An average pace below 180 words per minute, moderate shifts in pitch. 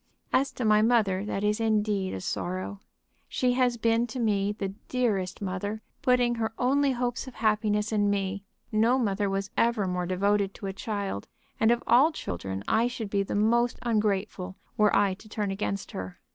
No: average, 185 wpm; average, 3.2 semitones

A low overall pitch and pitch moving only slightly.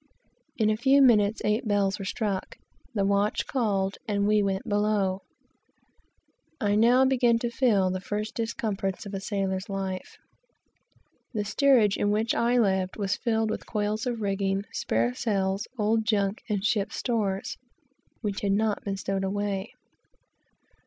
No: high, 205 Hz; narrow, 2.2 semitones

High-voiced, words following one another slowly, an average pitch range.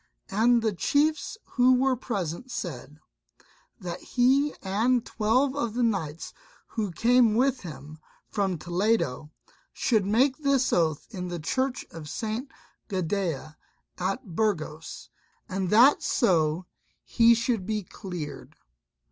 No: high, 210 Hz; slow, 120 wpm; wide, 6.0 semitones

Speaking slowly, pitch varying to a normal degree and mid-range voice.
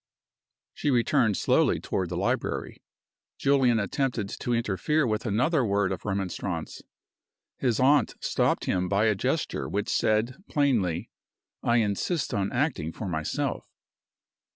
No: slow, 130 wpm; average, 4.7 semitones; low, 110 Hz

